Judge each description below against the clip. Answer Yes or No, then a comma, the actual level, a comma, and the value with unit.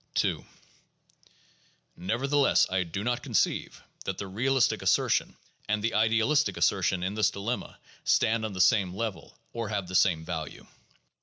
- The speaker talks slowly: No, average, 145 wpm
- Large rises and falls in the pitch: No, average, 3.7 semitones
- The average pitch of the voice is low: Yes, low, 105 Hz